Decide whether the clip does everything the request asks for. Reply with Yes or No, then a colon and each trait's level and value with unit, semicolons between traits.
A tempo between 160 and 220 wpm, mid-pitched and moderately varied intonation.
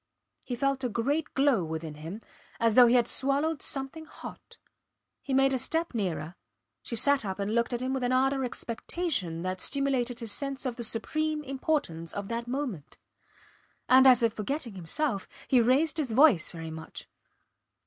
No: average, 180 wpm; very high, 250 Hz; average, 4.8 semitones